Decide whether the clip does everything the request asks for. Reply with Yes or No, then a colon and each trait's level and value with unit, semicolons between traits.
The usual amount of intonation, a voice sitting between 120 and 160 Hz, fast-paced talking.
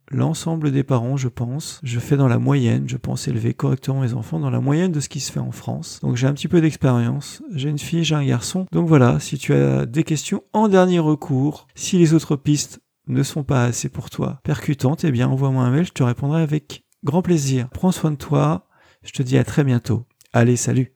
Yes: average, 3.7 semitones; medium, 140 Hz; fast, 235 wpm